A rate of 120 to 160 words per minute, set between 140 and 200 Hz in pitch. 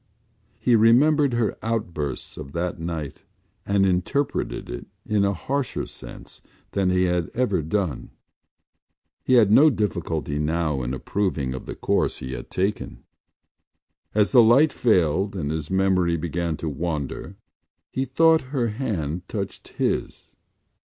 No: average, 140 wpm; very low, 95 Hz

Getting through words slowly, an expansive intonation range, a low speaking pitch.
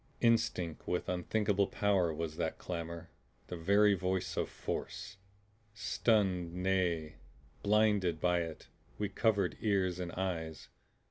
No: slow, 120 wpm; average, 3.1 semitones; very low, 90 Hz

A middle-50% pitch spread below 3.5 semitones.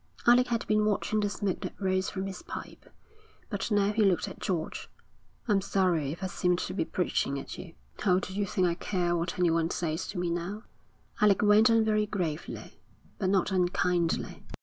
Yes: average, 2.9 semitones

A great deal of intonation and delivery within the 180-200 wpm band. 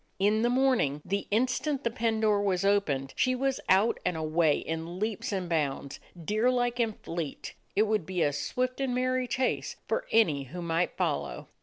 Yes: wide, 6.9 semitones; average, 185 wpm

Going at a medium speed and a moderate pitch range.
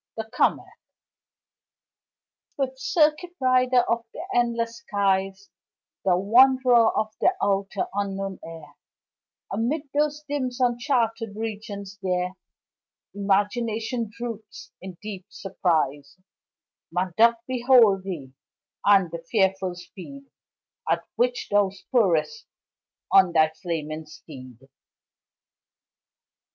No: slow, 95 wpm; average, 4.6 semitones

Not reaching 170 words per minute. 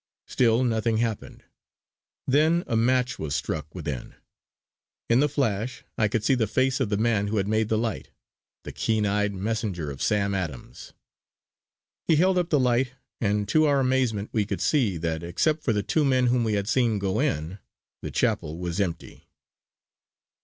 No: average, 175 wpm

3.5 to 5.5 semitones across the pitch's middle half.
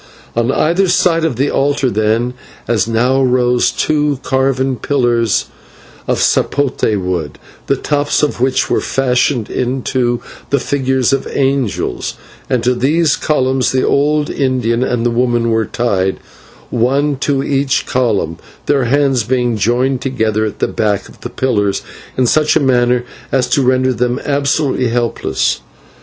No: average, 2.7 semitones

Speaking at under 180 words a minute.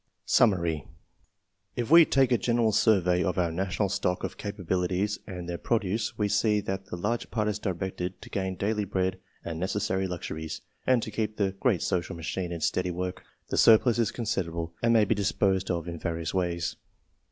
No: average, 185 wpm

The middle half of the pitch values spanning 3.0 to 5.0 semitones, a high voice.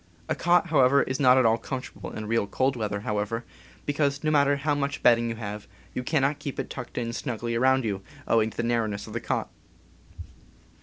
No: average, 3.8 semitones; low, 125 Hz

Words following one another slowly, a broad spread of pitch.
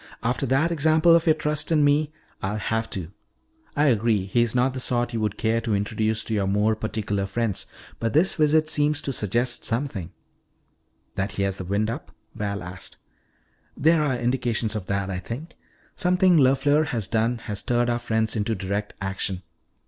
No: average, 185 wpm; wide, 5.7 semitones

